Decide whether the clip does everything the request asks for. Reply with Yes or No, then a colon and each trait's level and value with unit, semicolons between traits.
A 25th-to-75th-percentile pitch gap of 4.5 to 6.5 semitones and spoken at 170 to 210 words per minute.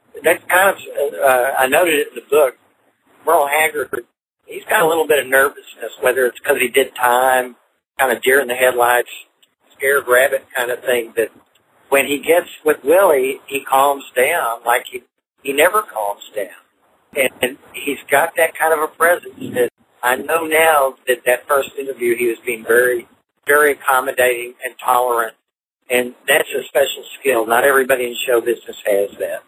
Yes: average, 5.2 semitones; average, 180 wpm